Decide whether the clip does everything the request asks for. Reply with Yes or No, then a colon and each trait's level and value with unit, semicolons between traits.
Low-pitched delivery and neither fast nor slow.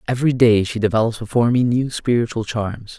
Yes: low, 115 Hz; average, 180 wpm